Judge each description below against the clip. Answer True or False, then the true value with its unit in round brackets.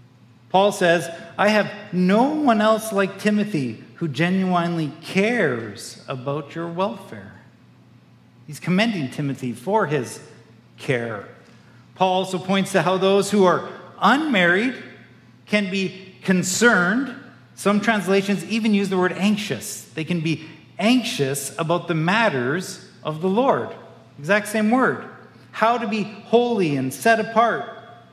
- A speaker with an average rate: False (130 wpm)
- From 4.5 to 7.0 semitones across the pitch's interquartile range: True (5.6 semitones)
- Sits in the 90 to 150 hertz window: False (185 Hz)